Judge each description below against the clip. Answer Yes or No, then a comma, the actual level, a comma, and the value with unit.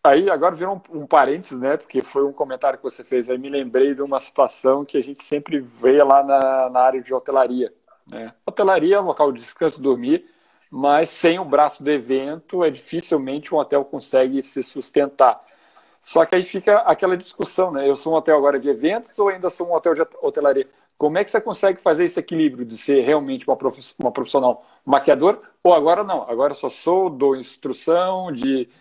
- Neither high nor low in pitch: Yes, medium, 145 Hz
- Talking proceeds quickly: Yes, fast, 210 wpm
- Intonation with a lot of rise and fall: No, average, 4.8 semitones